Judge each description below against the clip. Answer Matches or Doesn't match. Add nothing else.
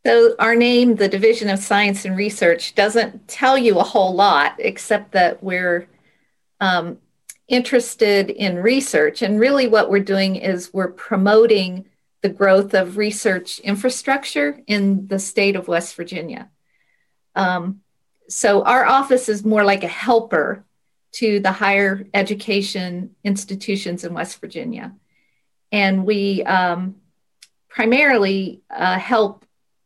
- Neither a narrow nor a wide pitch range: Matches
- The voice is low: Doesn't match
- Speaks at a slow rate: Matches